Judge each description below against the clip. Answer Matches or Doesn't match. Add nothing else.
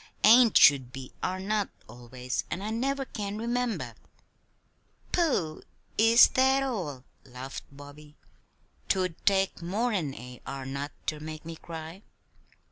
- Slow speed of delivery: Matches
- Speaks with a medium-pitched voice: Matches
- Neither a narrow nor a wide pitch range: Doesn't match